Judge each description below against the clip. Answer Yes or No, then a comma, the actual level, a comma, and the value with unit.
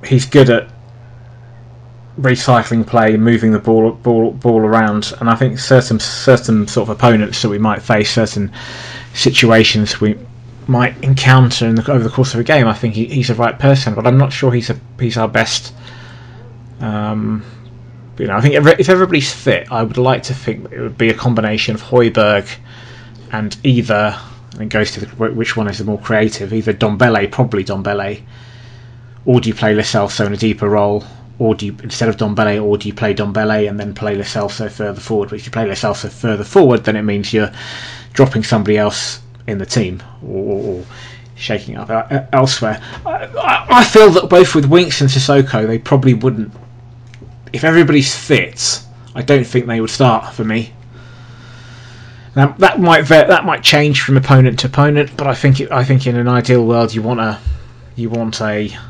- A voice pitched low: Yes, low, 120 Hz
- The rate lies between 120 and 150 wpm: No, average, 190 wpm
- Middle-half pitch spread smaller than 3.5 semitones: Yes, narrow, 2.5 semitones